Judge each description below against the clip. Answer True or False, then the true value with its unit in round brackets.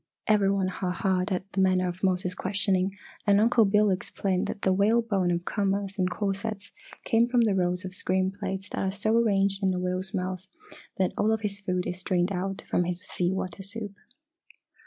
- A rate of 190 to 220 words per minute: True (200 wpm)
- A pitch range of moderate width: False (1.7 semitones)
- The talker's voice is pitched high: True (195 Hz)